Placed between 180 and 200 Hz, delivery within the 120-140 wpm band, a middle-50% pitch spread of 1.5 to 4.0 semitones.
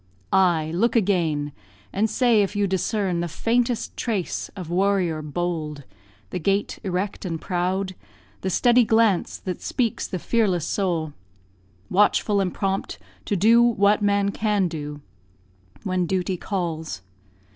Yes: high, 190 Hz; slow, 135 wpm; average, 3.1 semitones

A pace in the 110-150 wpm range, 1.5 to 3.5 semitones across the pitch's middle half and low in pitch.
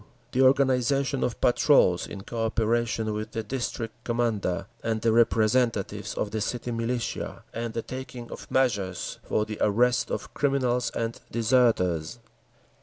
Yes: average, 140 wpm; narrow, 2.4 semitones; low, 115 Hz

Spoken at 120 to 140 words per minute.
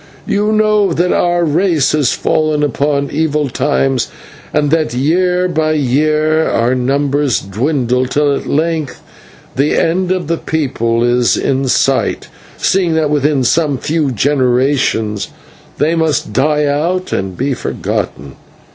Yes: slow, 135 wpm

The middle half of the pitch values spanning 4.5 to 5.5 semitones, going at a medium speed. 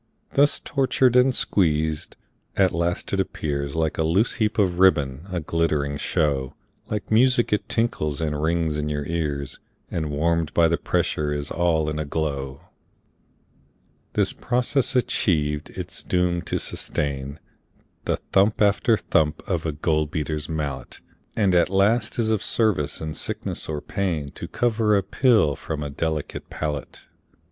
Yes: average, 4.9 semitones; average, 155 wpm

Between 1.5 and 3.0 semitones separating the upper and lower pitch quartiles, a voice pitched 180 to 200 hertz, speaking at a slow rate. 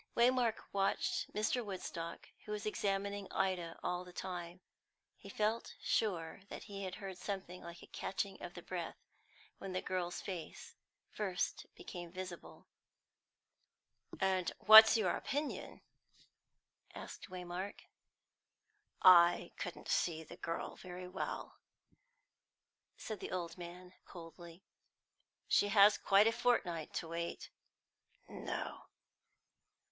Yes: narrow, 2.6 semitones; medium, 185 Hz; slow, 115 wpm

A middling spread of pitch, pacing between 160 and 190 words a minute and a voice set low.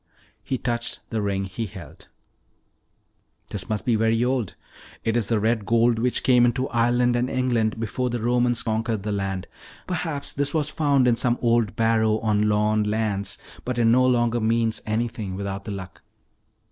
No: narrow, 2.3 semitones; average, 170 wpm; low, 115 Hz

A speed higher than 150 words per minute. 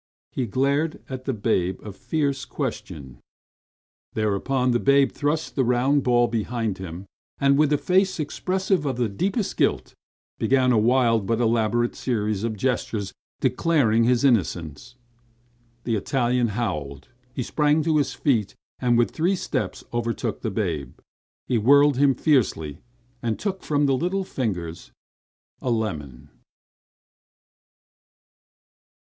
No: slow, 135 wpm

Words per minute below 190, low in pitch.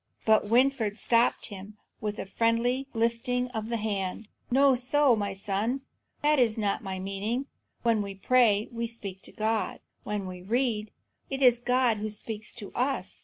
No: average, 170 wpm; high, 225 Hz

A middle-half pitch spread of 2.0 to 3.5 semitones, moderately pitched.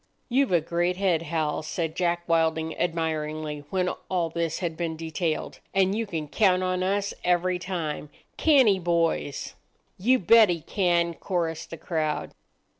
Yes: narrow, 2.4 semitones; medium, 170 Hz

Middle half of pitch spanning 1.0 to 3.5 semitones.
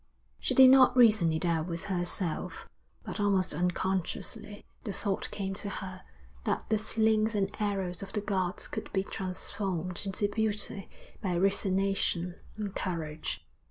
Yes: narrow, 2.4 semitones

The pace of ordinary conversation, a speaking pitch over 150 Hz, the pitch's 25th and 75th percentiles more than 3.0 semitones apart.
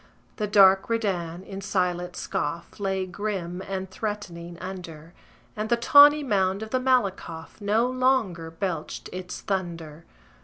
No: slow, 130 wpm; high, 190 Hz; average, 3.5 semitones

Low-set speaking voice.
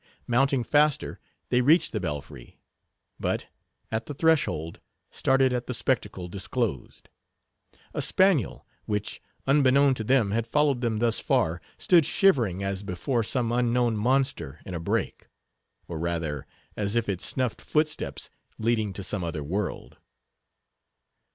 Yes: low, 115 Hz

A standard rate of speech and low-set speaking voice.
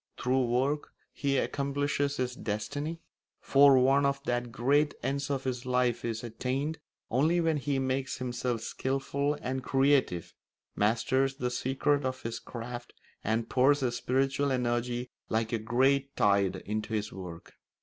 Yes: average, 145 wpm; low, 130 Hz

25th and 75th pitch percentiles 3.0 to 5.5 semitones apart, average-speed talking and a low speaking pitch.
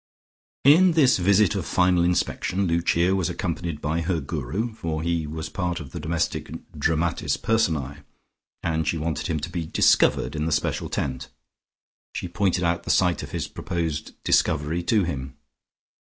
No: narrow, 2.5 semitones; average, 160 wpm; very low, 85 Hz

